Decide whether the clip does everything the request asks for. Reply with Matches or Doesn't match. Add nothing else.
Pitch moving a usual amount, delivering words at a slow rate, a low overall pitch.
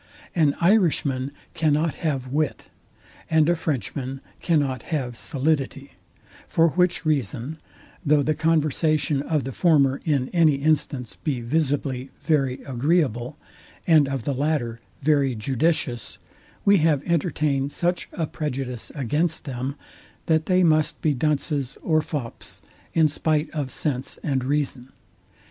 Doesn't match